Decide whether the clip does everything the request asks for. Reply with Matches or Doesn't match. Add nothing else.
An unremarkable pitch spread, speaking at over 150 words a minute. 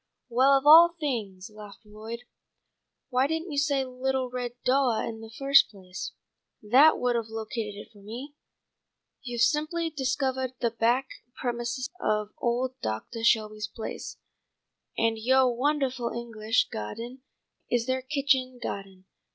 Doesn't match